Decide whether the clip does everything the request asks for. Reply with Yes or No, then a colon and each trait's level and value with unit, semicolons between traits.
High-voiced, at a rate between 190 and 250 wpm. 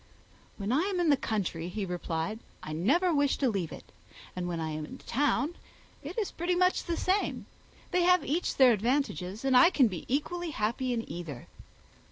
Yes: very high, 250 Hz; average, 195 wpm